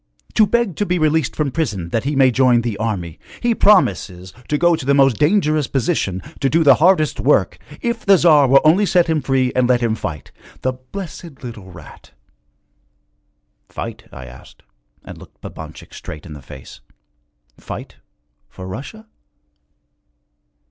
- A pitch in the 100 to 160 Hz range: Yes, low, 135 Hz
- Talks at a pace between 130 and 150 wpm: No, average, 160 wpm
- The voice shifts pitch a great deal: Yes, wide, 7.1 semitones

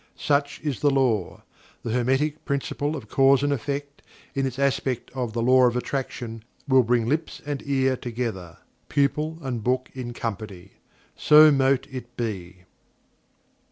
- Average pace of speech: Yes, average, 150 wpm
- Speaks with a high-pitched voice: No, low, 130 Hz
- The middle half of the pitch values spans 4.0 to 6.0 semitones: No, average, 3.0 semitones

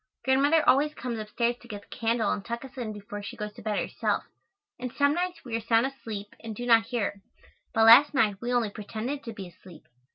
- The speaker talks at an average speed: No, fast, 230 wpm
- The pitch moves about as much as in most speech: Yes, average, 3.7 semitones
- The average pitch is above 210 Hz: Yes, high, 230 Hz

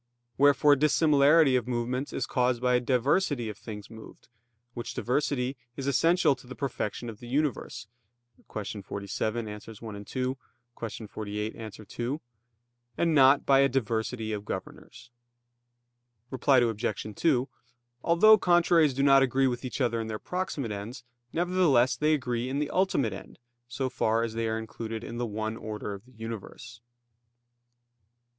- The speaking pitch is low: Yes, low, 125 Hz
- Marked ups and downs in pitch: No, average, 3.8 semitones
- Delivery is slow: No, average, 150 wpm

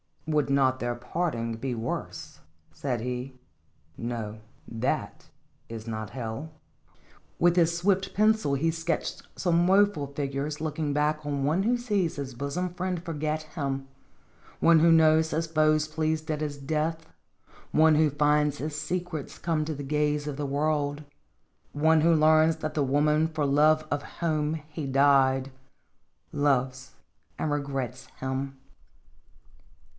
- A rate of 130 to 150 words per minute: Yes, average, 140 wpm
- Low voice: No, medium, 150 Hz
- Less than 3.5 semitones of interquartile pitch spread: Yes, average, 2.8 semitones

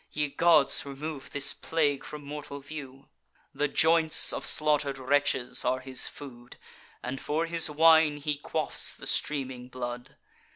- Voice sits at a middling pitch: Yes, medium, 145 Hz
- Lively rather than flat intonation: No, narrow, 2.5 semitones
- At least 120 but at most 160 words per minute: Yes, average, 140 wpm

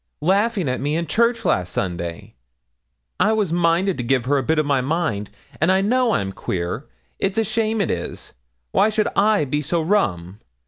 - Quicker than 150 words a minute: Yes, average, 190 wpm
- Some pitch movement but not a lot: No, wide, 8.7 semitones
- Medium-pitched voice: Yes, medium, 165 Hz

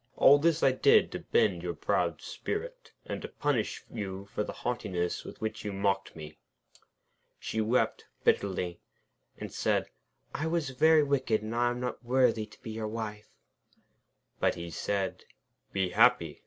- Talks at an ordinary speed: Yes, average, 160 wpm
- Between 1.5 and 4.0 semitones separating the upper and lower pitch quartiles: No, average, 5.2 semitones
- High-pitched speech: No, low, 110 Hz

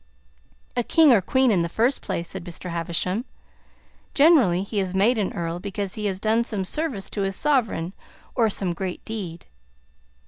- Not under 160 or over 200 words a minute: Yes, average, 175 wpm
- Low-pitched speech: No, high, 200 Hz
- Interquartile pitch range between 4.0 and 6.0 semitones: Yes, average, 4.5 semitones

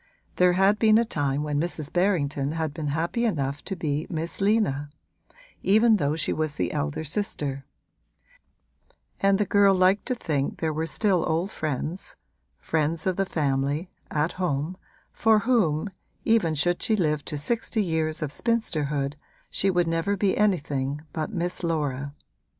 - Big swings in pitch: No, average, 5.0 semitones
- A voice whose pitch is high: No, medium, 165 Hz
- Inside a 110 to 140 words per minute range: No, average, 155 wpm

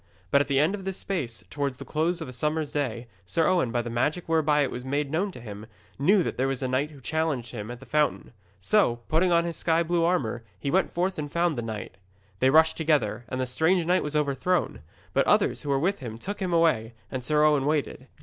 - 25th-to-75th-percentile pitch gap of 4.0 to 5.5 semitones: Yes, average, 4.9 semitones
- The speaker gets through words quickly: Yes, fast, 245 wpm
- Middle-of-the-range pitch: Yes, medium, 150 Hz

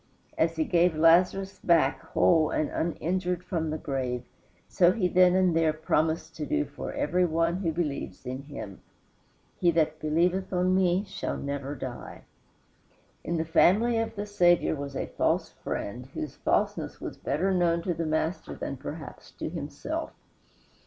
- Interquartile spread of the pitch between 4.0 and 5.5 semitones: No, average, 2.8 semitones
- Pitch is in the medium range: Yes, medium, 165 Hz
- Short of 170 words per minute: Yes, average, 160 wpm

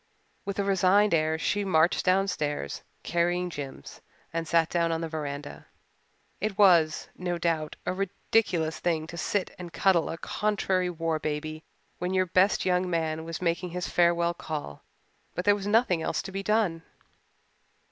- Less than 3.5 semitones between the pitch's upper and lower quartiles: Yes, average, 2.8 semitones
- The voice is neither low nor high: Yes, medium, 175 Hz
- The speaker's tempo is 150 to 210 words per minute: Yes, average, 160 wpm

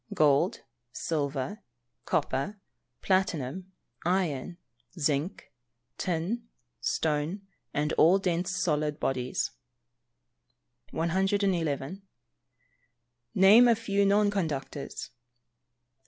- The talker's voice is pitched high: No, medium, 170 Hz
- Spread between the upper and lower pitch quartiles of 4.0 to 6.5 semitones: Yes, average, 4.8 semitones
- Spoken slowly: Yes, slow, 75 wpm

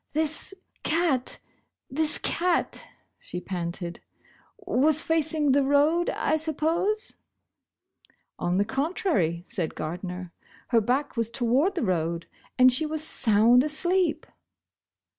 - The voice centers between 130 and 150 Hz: No, very high, 275 Hz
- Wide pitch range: Yes, wide, 7.8 semitones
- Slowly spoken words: Yes, slow, 120 wpm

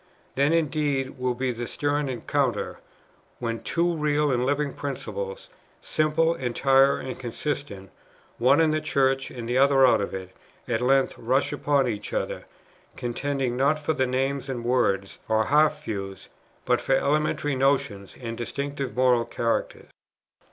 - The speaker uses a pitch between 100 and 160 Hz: Yes, low, 135 Hz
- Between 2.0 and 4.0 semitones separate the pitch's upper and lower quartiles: Yes, average, 3.2 semitones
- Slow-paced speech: No, average, 145 wpm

